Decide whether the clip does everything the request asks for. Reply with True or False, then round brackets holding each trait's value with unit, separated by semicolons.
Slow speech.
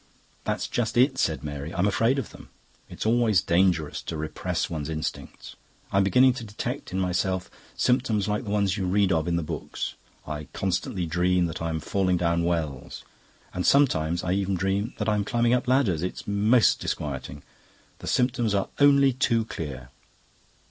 False (170 wpm)